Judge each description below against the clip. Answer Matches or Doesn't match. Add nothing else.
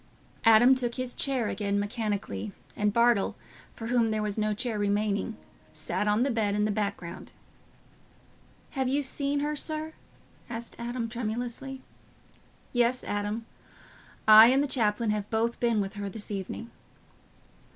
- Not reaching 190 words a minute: Matches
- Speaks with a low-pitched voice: Doesn't match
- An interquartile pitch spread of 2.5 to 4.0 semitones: Matches